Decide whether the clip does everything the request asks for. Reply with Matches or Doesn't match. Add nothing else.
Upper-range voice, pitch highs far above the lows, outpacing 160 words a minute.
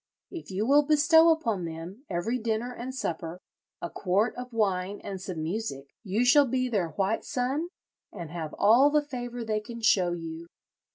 Matches